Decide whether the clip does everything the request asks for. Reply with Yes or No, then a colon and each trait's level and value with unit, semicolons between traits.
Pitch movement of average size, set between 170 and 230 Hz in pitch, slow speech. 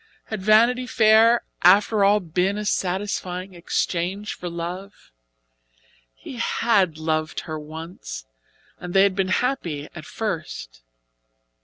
Yes: average, 3.9 semitones; medium, 185 Hz; slow, 120 wpm